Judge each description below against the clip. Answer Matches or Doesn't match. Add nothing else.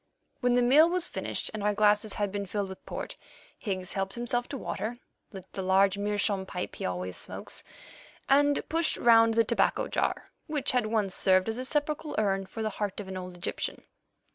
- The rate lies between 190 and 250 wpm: Matches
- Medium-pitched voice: Doesn't match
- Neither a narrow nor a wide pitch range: Matches